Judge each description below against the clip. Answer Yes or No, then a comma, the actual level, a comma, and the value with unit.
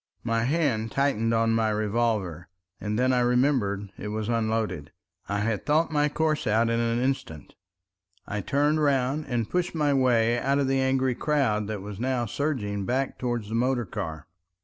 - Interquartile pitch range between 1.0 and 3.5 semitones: No, average, 4.0 semitones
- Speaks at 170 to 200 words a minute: Yes, average, 175 wpm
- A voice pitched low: Yes, low, 120 Hz